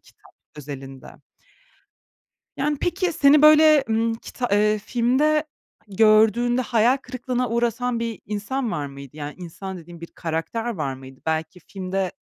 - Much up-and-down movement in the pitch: Yes, wide, 6.9 semitones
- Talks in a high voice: Yes, high, 220 Hz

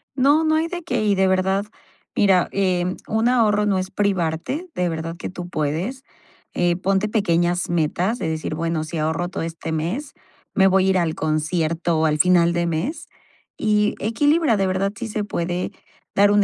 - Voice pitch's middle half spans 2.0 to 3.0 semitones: No, average, 4.0 semitones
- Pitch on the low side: No, medium, 185 Hz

